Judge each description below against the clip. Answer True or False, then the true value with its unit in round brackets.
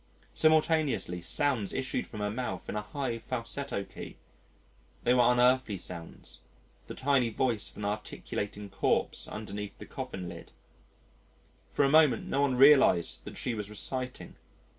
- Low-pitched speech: True (120 Hz)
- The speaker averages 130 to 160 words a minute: True (145 wpm)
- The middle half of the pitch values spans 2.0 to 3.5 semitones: False (4.5 semitones)